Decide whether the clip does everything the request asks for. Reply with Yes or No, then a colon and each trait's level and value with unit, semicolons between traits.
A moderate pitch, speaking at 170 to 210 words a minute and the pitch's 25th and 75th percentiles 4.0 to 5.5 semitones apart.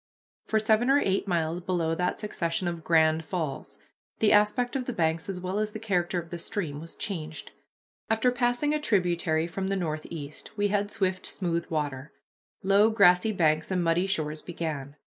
Yes: medium, 180 Hz; average, 180 wpm; average, 4.3 semitones